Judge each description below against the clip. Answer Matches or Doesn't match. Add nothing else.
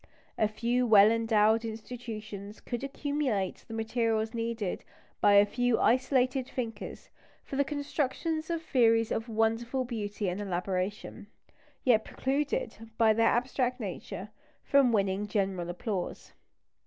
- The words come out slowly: Matches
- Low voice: Doesn't match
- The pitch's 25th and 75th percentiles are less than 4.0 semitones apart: Matches